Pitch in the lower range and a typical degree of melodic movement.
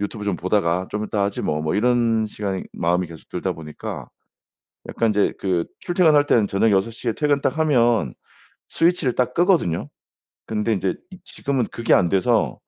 Yes: low, 105 Hz; average, 5.0 semitones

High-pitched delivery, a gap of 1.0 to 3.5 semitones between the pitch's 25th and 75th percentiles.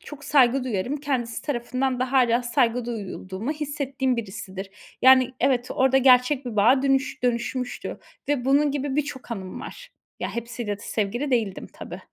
Yes: very high, 250 Hz; narrow, 2.6 semitones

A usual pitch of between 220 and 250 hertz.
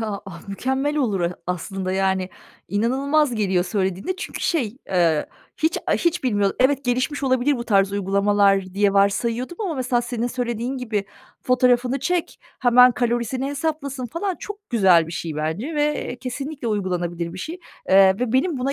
Yes: high, 240 Hz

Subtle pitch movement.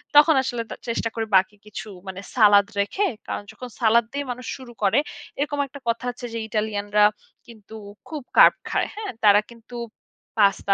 No: average, 3.6 semitones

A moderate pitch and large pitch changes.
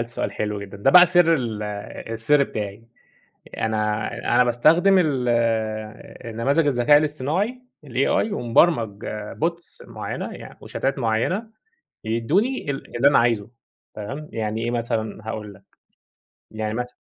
No: low, 120 Hz; wide, 5.7 semitones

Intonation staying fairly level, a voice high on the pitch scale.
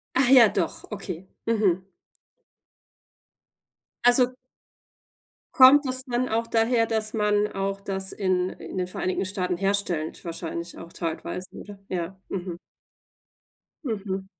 No: average, 3.8 semitones; high, 195 Hz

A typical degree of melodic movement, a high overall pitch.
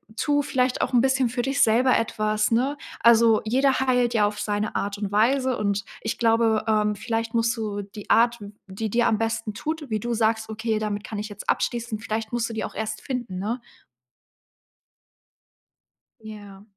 No: narrow, 2.2 semitones; high, 225 Hz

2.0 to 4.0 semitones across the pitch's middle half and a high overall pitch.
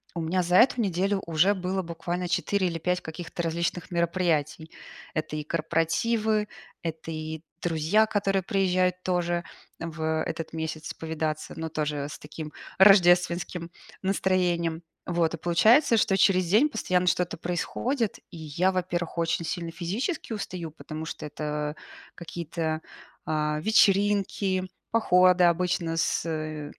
No: average, 2.7 semitones; medium, 175 Hz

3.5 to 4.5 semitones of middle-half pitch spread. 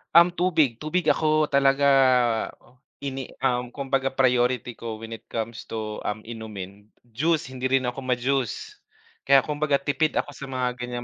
No: average, 3.0 semitones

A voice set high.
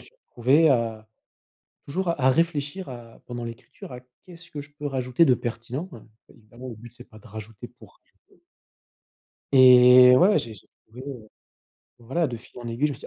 No: low, 125 Hz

